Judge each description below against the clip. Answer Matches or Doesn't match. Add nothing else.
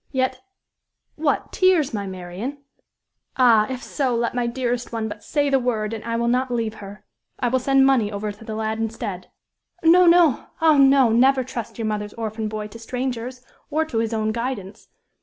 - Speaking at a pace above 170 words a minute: Matches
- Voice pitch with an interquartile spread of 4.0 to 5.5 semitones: Doesn't match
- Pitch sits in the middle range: Doesn't match